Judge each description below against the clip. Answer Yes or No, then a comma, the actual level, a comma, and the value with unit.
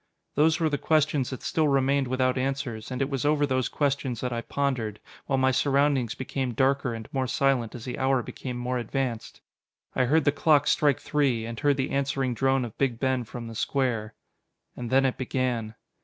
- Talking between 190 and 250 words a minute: Yes, average, 200 wpm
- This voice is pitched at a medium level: No, low, 130 Hz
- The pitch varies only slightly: Yes, narrow, 2.3 semitones